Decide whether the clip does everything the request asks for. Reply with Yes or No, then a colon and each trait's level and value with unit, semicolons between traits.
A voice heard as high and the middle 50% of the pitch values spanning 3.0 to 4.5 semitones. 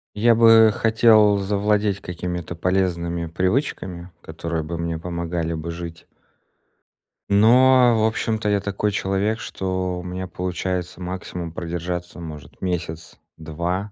No: very low, 90 Hz; average, 3.4 semitones